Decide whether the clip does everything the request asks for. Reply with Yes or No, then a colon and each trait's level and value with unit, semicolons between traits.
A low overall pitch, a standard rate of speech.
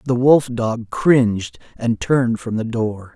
Yes: low, 120 Hz; average, 170 wpm